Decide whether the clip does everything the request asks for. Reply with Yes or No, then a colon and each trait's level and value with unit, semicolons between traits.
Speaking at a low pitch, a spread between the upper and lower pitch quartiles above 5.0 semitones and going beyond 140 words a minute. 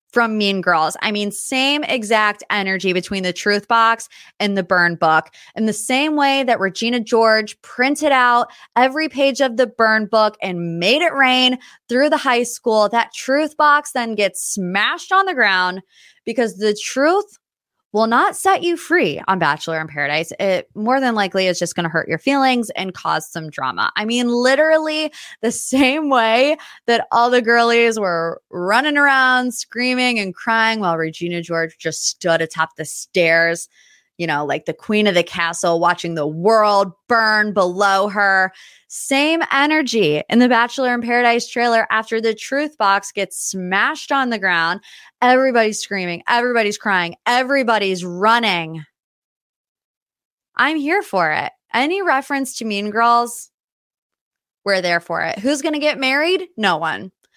No: high, 225 Hz; wide, 5.6 semitones; average, 165 wpm